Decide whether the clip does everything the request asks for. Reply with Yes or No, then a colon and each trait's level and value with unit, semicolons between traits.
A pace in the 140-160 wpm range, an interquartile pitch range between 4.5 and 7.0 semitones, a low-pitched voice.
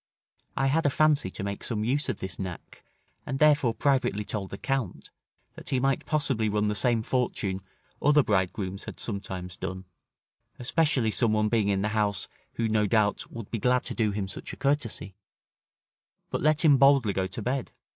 No: average, 185 wpm; average, 5.2 semitones; low, 110 Hz